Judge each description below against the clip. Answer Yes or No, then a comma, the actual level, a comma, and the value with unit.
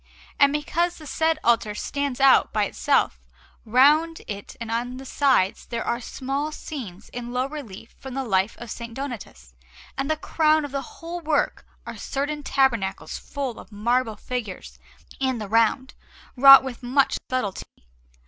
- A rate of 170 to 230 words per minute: No, average, 160 wpm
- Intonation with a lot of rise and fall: No, average, 3.7 semitones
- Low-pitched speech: No, very high, 260 Hz